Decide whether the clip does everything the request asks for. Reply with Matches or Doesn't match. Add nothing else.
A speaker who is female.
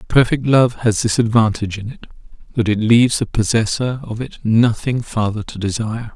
Doesn't match